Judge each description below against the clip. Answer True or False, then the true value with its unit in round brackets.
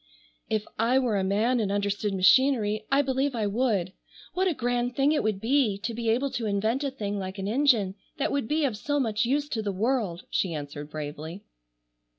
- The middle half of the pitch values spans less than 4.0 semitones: False (4.8 semitones)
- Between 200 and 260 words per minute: True (205 wpm)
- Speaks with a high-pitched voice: True (220 Hz)